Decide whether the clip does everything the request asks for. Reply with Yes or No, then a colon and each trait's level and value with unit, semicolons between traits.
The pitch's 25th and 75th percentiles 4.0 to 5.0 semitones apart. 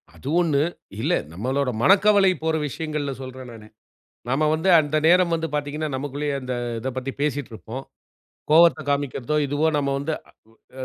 No: average, 3.2 semitones